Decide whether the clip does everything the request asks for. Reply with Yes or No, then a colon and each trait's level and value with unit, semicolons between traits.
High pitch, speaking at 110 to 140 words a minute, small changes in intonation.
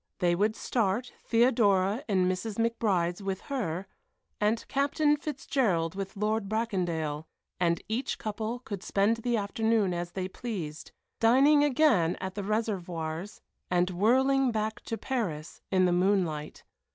No: high, 205 Hz; slow, 135 wpm; average, 4.3 semitones